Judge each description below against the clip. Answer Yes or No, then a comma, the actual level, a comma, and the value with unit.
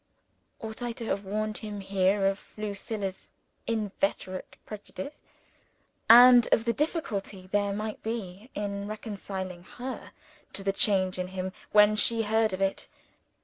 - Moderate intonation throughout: No, narrow, 2.3 semitones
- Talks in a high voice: Yes, high, 205 Hz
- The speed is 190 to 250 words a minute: No, average, 140 wpm